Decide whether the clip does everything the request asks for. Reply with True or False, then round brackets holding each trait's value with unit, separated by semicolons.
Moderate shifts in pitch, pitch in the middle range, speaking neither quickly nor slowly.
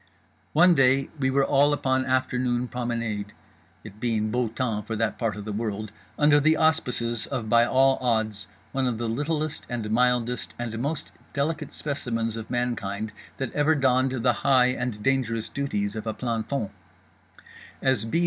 False (3.2 semitones; 125 Hz; 165 wpm)